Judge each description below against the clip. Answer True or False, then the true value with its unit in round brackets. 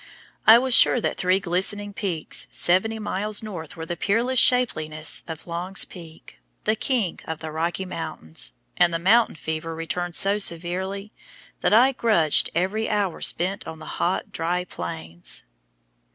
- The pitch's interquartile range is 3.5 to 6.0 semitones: True (4.2 semitones)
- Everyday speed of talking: True (150 wpm)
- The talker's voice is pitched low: False (180 Hz)